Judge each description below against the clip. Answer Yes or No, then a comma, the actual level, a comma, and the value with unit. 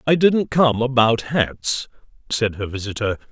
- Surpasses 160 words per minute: No, average, 145 wpm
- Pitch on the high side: No, low, 125 Hz